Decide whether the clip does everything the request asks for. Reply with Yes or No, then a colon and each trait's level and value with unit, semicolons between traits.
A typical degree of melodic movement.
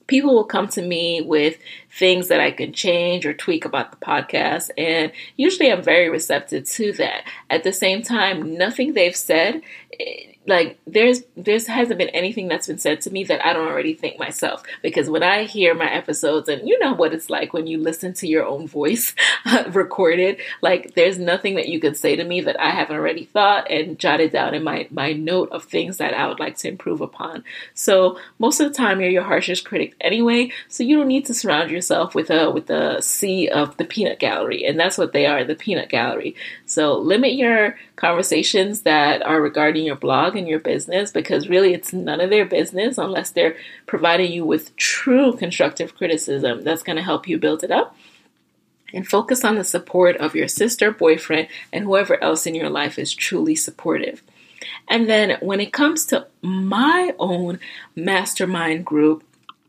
No: wide, 5.8 semitones